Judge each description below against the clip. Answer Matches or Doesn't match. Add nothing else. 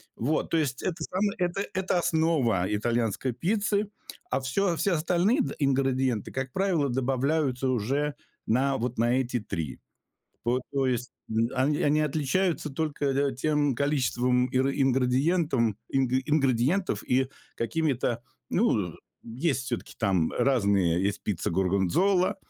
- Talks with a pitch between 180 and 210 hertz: Doesn't match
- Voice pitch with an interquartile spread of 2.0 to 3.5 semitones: Doesn't match